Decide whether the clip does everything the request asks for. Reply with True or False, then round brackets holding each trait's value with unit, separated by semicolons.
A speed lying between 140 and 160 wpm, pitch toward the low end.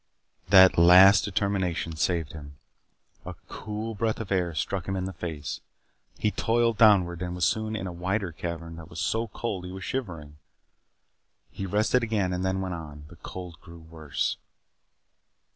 False (170 wpm; 90 Hz)